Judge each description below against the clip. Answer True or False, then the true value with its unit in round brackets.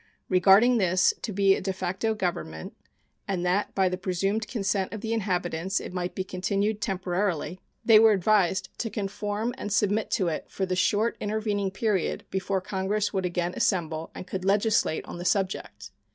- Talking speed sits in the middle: True (175 wpm)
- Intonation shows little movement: True (2.3 semitones)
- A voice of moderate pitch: False (195 Hz)